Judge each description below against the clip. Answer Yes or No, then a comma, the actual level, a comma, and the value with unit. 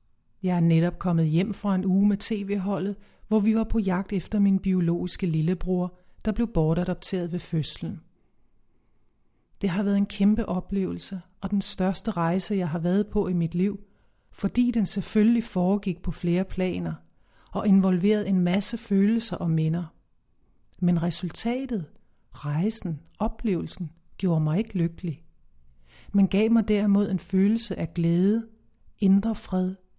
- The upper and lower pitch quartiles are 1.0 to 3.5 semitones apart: Yes, average, 2.9 semitones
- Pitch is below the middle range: No, medium, 185 Hz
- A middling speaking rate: Yes, average, 145 wpm